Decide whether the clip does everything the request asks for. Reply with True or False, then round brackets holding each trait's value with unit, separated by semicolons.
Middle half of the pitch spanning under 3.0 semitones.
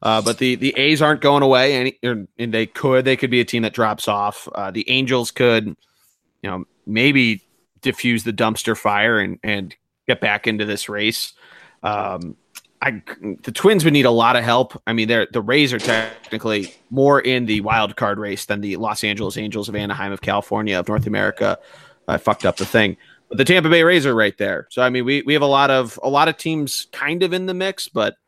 False (4.2 semitones)